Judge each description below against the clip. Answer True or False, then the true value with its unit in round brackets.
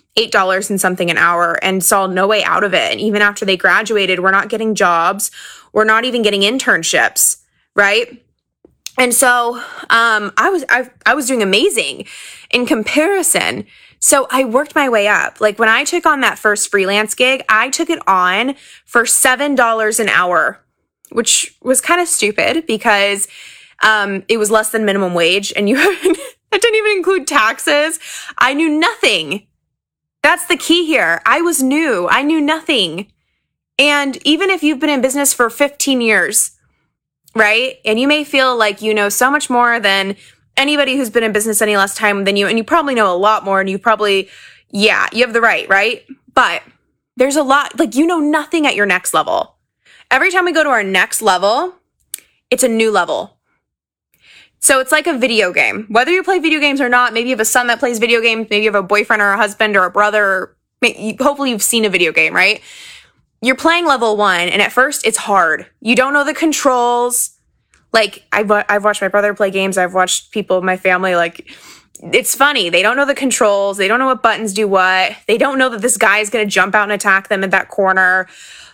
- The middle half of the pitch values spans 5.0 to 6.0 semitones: True (5.6 semitones)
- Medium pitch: False (230 Hz)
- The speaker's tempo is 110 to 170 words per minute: False (205 wpm)